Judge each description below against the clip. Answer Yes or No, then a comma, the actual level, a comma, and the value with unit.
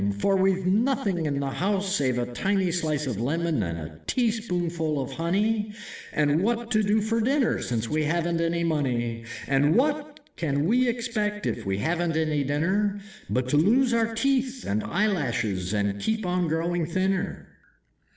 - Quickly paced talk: No, average, 165 wpm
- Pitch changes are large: Yes, wide, 6.9 semitones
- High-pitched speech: No, medium, 175 Hz